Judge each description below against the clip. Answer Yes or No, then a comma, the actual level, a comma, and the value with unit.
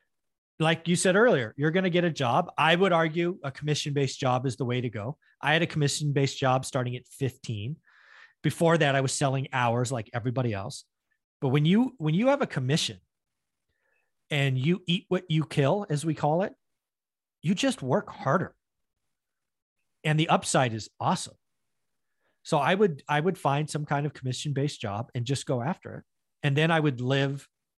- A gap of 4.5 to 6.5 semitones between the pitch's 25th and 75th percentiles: No, average, 4.0 semitones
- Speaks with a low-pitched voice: No, medium, 145 Hz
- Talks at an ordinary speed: Yes, average, 190 wpm